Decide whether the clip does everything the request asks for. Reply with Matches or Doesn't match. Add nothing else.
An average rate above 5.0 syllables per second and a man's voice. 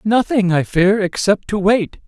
Doesn't match